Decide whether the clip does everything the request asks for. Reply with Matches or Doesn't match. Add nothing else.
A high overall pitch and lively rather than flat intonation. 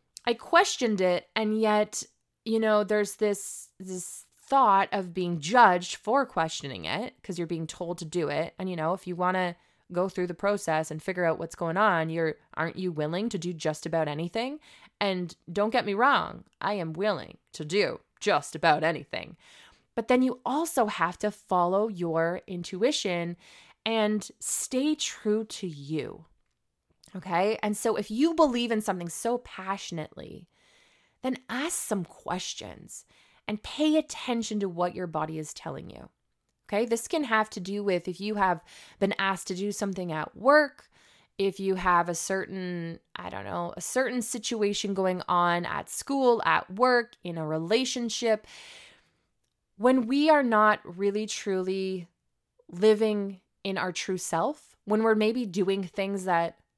Doesn't match